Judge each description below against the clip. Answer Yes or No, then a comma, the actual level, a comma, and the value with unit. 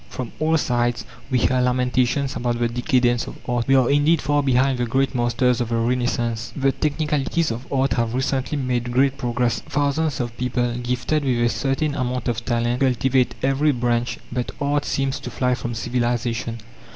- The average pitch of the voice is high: No, low, 125 Hz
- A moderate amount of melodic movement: No, narrow, 2.2 semitones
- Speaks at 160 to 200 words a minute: Yes, average, 180 wpm